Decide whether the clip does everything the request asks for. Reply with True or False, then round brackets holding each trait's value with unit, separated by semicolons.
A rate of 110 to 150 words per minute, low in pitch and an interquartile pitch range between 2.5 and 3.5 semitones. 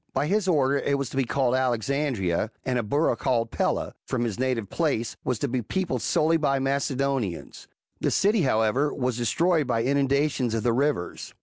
False (190 wpm; 130 Hz; 3.2 semitones)